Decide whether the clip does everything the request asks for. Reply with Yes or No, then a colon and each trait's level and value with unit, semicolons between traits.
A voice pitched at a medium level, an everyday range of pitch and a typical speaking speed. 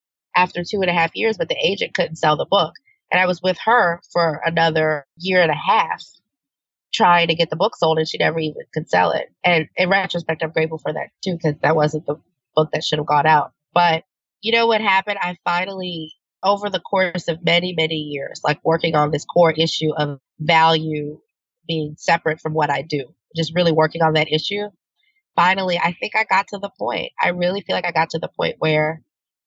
No: medium, 165 Hz; average, 3.0 semitones; fast, 220 wpm